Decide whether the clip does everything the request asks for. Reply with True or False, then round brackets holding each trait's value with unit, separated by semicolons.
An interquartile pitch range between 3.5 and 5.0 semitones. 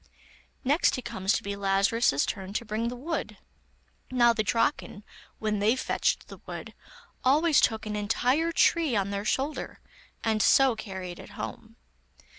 True (4.2 semitones)